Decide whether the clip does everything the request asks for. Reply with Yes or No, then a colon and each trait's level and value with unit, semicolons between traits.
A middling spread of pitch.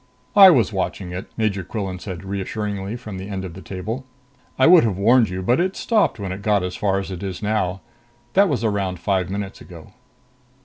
Yes: average, 3.0 semitones